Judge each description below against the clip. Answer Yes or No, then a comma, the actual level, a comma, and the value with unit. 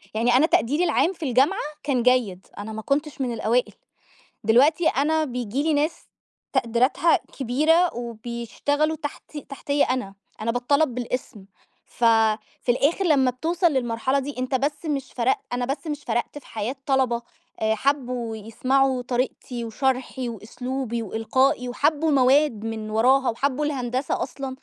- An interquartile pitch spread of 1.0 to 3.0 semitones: No, average, 3.4 semitones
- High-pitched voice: Yes, very high, 260 Hz